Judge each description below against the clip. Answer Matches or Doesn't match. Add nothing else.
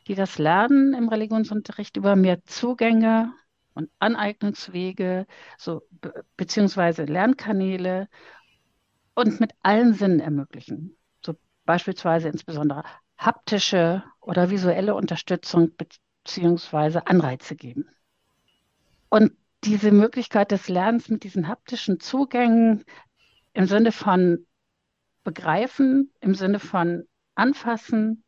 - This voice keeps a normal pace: Doesn't match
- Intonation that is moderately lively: Matches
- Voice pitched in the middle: Doesn't match